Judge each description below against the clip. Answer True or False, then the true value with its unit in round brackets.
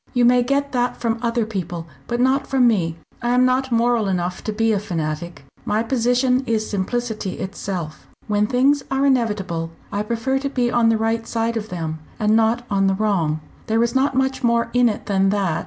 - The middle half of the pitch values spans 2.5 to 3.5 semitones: False (3.9 semitones)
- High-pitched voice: True (225 Hz)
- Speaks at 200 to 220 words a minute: True (205 wpm)